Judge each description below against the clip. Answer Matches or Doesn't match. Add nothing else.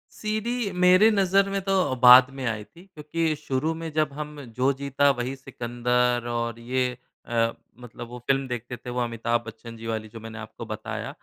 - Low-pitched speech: Matches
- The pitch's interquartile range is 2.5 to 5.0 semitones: Matches